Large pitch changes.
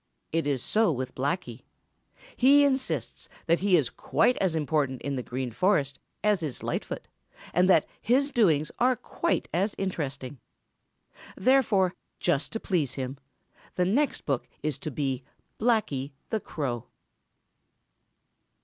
Yes: wide, 7.4 semitones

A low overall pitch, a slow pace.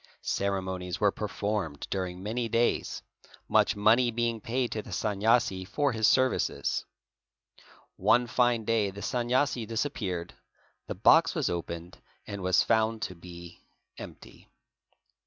Yes: low, 105 Hz; slow, 125 wpm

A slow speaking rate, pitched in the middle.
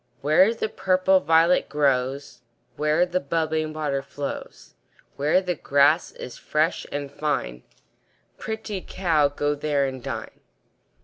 Yes: slow, 125 wpm; medium, 150 Hz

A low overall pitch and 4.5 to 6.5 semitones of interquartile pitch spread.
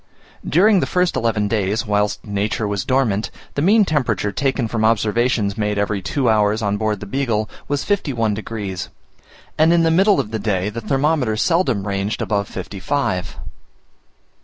Yes: low, 110 Hz; average, 5.2 semitones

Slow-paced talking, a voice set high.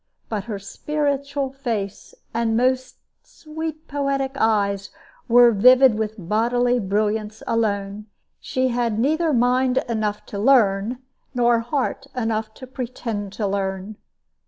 Yes: slow, 120 wpm; high, 235 Hz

